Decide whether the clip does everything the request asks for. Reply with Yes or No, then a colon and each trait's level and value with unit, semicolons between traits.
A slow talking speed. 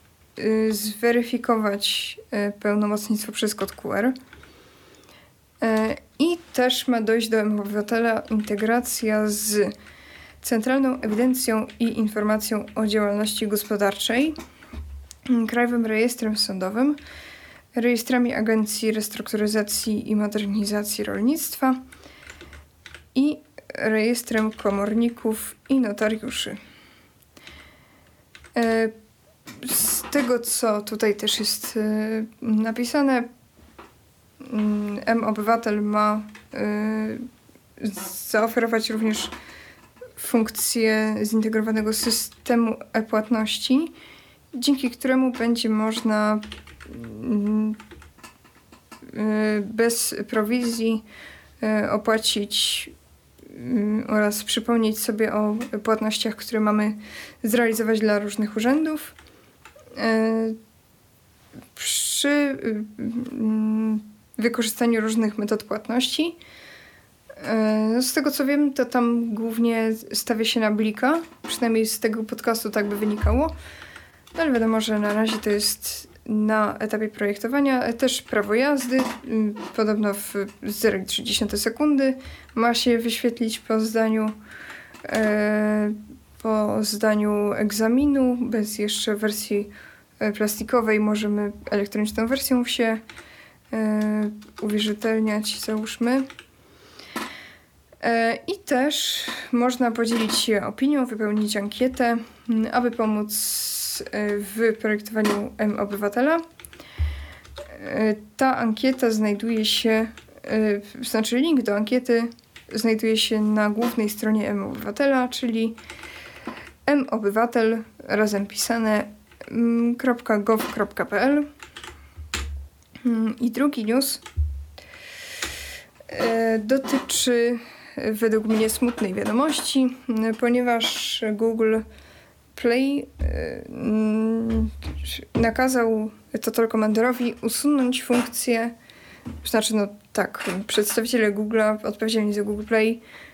Yes: slow, 80 wpm